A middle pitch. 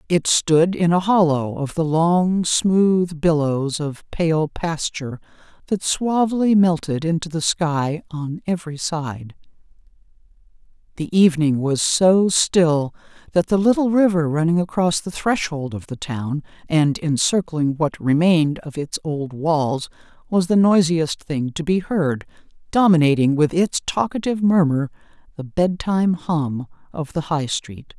Yes: medium, 165 Hz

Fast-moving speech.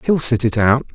Yes: fast, 255 wpm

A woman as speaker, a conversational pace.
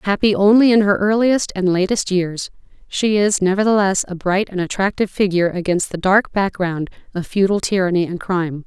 Yes: female; average, 175 wpm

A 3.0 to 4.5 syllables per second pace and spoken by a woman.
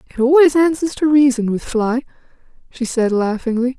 No: 5.1 syllables/s; female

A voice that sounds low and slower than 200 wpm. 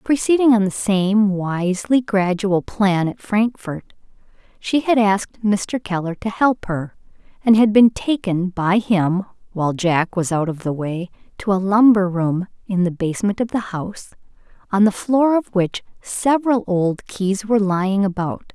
No: high, 200 Hz; average, 165 wpm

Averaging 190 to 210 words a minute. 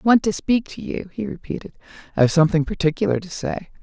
Yes: fast, 205 wpm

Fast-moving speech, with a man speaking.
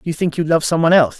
Yes: fast, 300 wpm; male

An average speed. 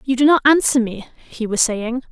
No: fast, 225 wpm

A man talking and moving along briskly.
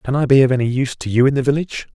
Yes: male; fast, 330 wpm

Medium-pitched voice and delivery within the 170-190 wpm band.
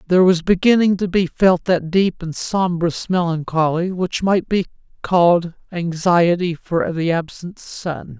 No: medium, 175 Hz; average, 145 wpm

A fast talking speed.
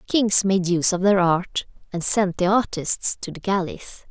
No: average, 190 wpm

